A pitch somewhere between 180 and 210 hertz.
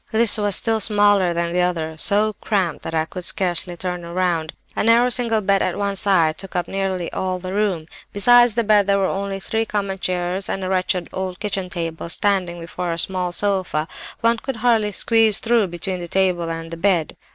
Yes: high, 190 Hz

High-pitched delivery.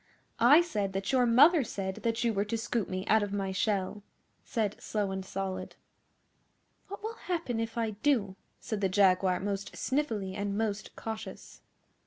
Yes: high, 210 Hz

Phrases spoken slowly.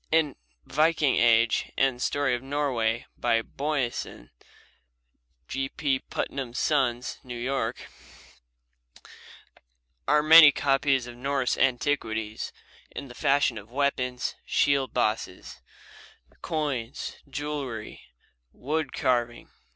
Yes: slow, 95 wpm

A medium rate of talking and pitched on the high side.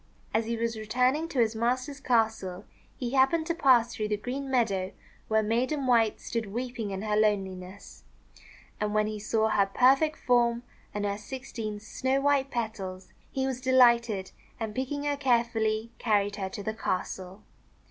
Yes: average, 170 wpm; high, 230 Hz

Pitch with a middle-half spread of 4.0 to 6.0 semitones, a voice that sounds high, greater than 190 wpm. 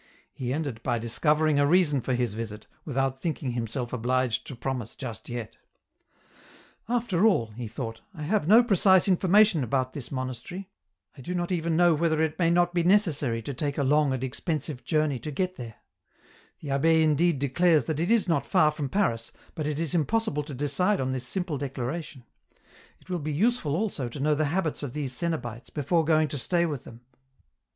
No: average, 4.9 semitones; medium, 150 Hz; average, 200 wpm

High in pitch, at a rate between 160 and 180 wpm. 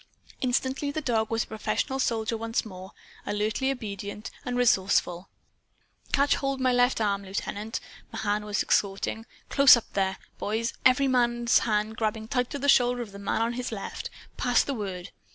Yes: high, 225 Hz; average, 170 wpm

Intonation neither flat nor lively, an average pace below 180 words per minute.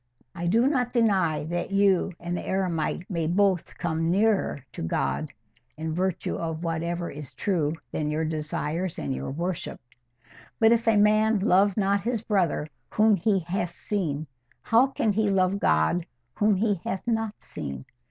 Yes: average, 4.4 semitones; average, 160 wpm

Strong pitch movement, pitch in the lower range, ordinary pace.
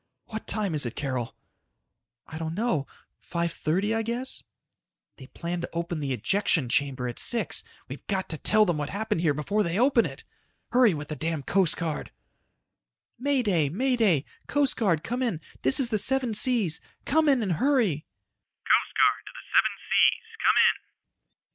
No: wide, 7.2 semitones; medium, 185 Hz; average, 155 wpm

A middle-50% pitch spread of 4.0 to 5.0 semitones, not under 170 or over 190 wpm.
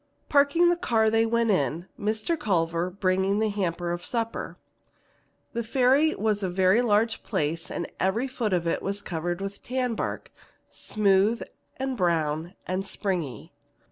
No: average, 4.6 semitones; average, 150 wpm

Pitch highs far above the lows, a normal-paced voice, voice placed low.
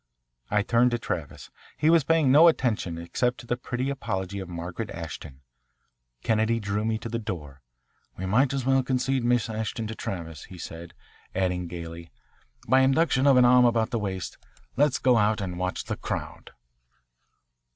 Yes: wide, 5.7 semitones; average, 170 wpm; low, 110 Hz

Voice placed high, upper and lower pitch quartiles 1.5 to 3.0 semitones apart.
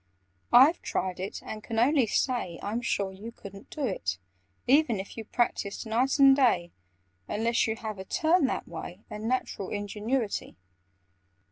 No: high, 220 Hz; average, 4.4 semitones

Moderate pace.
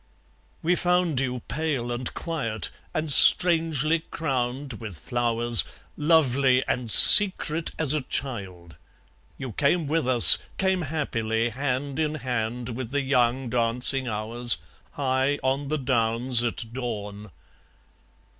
No: slow, 120 wpm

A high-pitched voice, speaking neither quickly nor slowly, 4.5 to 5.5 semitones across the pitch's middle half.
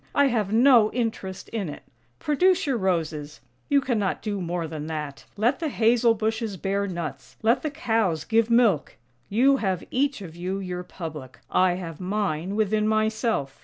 Yes: high, 205 Hz; average, 175 wpm; average, 4.9 semitones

